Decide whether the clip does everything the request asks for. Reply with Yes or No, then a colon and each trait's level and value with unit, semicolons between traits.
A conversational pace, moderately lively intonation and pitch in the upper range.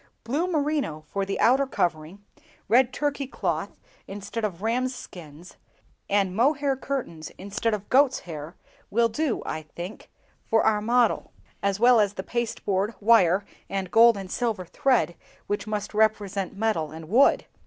Yes: average, 150 wpm; average, 4.3 semitones; high, 210 Hz